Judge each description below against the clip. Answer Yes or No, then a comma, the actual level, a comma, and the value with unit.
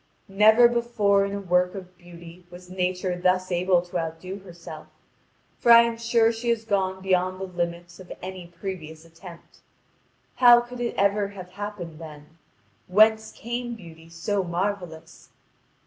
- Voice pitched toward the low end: No, medium, 185 Hz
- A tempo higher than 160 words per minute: No, average, 150 wpm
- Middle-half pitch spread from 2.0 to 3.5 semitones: Yes, average, 3.2 semitones